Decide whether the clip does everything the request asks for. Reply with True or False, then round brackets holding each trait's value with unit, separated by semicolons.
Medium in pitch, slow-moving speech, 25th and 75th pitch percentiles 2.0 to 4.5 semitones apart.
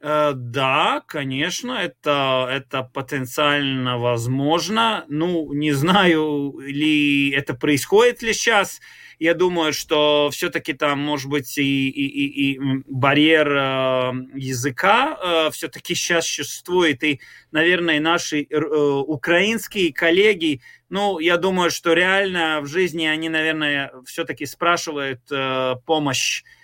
True (150 Hz; 105 wpm; 3.5 semitones)